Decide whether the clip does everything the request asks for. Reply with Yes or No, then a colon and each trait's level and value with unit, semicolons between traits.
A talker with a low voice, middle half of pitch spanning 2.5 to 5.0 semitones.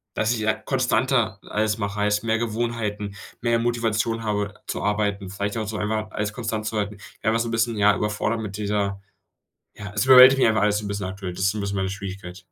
No: low, 105 Hz; narrow, 1.9 semitones